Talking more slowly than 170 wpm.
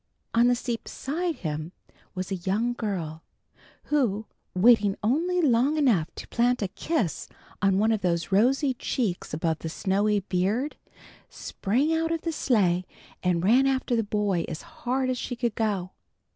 Yes: average, 160 wpm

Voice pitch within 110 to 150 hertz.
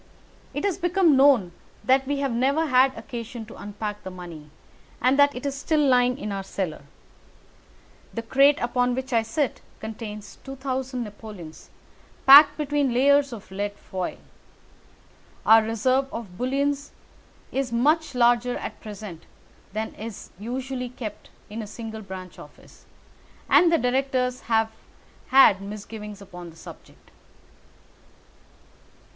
No: high, 245 Hz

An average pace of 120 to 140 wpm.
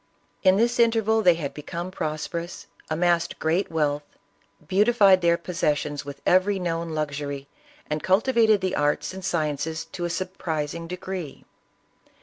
Yes: slow, 135 wpm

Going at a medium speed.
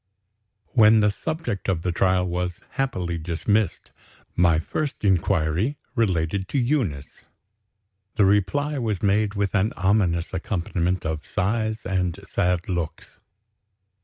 No: slow, 120 wpm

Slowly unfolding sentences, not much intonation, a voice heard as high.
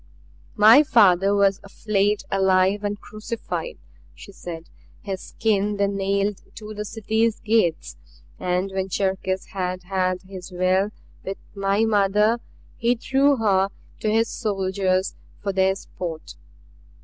Yes: slow, 125 wpm; narrow, 2.1 semitones; high, 195 Hz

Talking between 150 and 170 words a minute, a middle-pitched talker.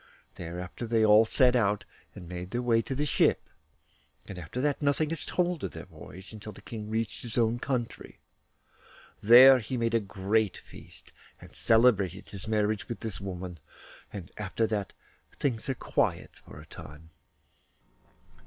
No: average, 165 wpm; low, 110 Hz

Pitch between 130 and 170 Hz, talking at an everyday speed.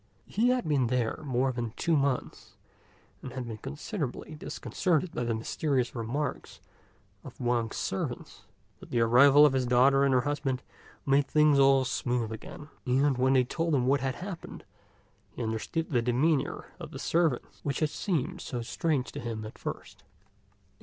Yes: low, 135 Hz; average, 165 wpm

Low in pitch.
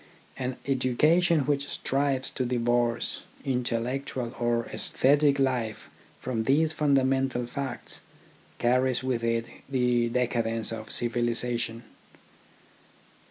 Yes: low, 125 Hz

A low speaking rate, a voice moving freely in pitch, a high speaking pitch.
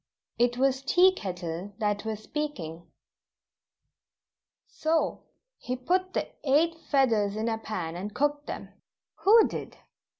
Yes: slow, 130 wpm; wide, 6.6 semitones; high, 245 Hz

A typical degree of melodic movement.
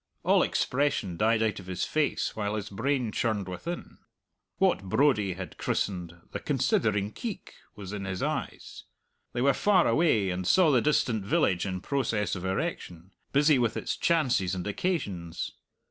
No: wide, 6.7 semitones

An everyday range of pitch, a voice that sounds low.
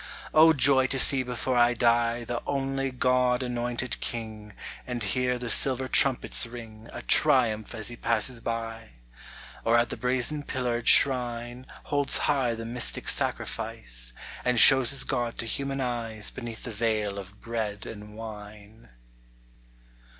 No: narrow, 2.2 semitones; low, 120 Hz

